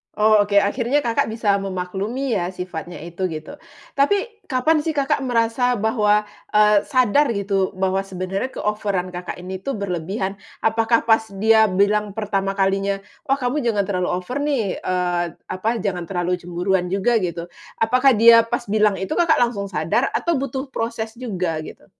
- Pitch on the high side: Yes, high, 210 Hz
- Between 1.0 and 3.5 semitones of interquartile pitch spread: No, average, 4.3 semitones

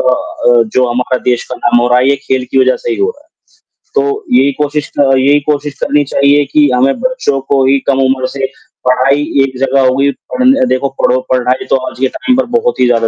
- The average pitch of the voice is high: No, low, 135 Hz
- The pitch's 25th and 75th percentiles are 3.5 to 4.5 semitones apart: No, narrow, 2.4 semitones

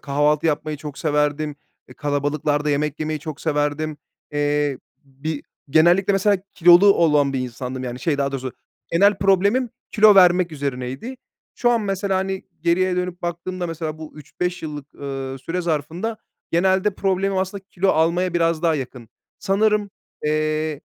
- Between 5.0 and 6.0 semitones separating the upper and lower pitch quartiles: No, average, 4.2 semitones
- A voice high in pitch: No, medium, 160 Hz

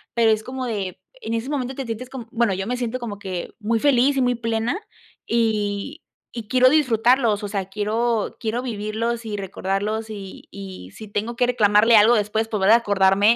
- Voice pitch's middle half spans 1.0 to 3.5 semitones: Yes, average, 2.7 semitones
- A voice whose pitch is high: Yes, high, 225 Hz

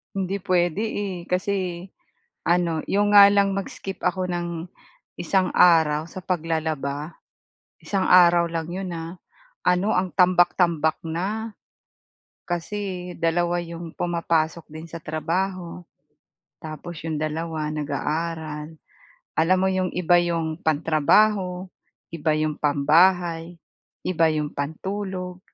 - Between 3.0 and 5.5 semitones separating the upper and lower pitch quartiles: No, narrow, 2.5 semitones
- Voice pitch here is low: No, medium, 175 Hz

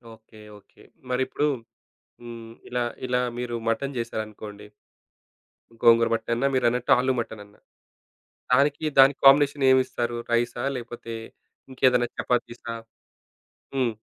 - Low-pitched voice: Yes, low, 120 Hz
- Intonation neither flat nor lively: No, narrow, 2.0 semitones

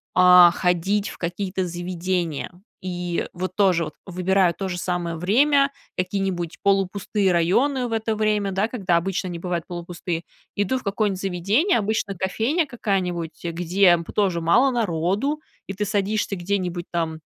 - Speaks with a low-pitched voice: No, medium, 185 Hz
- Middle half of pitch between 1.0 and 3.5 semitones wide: Yes, average, 2.9 semitones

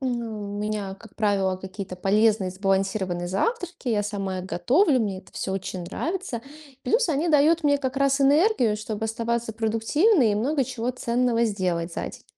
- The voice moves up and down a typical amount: No, wide, 5.7 semitones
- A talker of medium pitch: No, high, 220 Hz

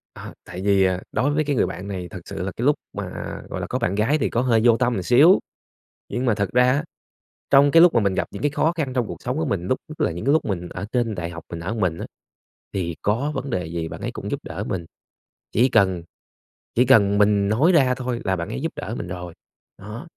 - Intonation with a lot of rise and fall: Yes, wide, 6.0 semitones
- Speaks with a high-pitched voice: No, low, 110 Hz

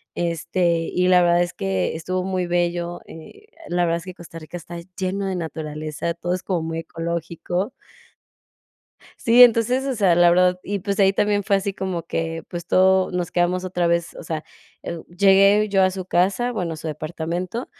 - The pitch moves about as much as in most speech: No, narrow, 2.2 semitones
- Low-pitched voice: No, medium, 175 Hz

